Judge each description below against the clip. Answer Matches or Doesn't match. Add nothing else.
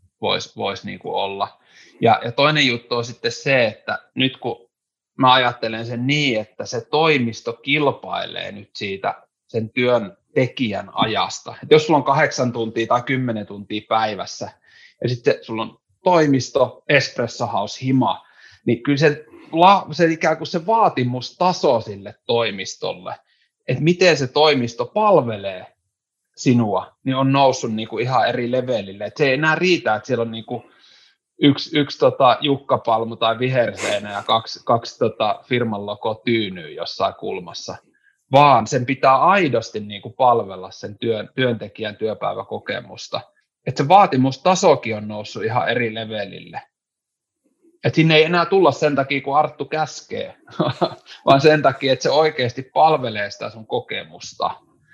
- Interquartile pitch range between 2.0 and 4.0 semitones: Doesn't match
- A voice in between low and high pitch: Doesn't match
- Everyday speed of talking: Matches